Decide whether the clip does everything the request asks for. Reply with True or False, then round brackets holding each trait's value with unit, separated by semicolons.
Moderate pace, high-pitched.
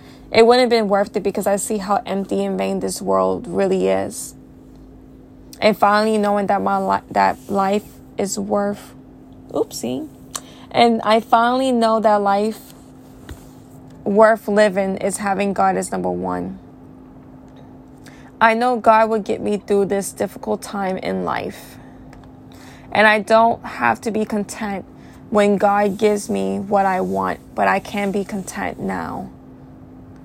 True (145 wpm; 200 Hz)